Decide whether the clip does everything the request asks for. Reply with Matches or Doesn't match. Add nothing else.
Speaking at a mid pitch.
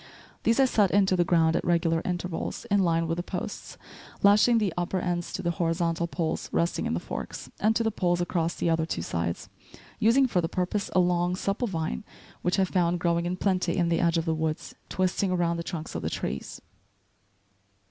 Matches